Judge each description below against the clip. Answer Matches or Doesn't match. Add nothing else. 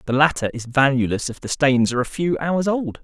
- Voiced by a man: Matches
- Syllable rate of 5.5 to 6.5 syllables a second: Matches